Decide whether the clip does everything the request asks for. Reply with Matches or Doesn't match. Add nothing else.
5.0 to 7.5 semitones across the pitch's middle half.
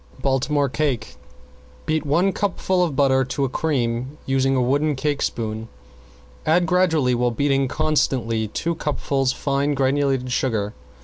Doesn't match